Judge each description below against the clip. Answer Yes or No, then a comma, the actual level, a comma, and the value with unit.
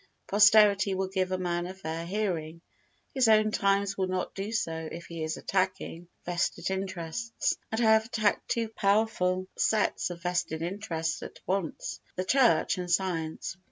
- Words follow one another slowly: No, average, 160 wpm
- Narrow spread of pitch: No, average, 3.4 semitones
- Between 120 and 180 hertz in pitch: No, high, 190 Hz